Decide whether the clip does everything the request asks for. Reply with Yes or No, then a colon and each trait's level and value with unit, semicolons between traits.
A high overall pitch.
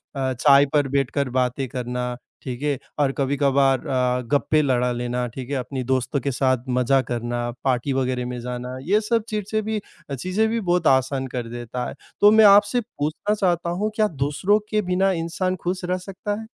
No: medium, 140 Hz